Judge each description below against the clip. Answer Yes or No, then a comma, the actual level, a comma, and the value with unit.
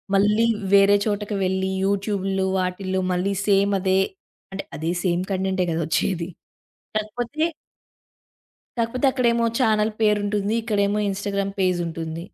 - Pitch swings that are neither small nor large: No, narrow, 2.1 semitones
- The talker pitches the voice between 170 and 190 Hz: No, high, 200 Hz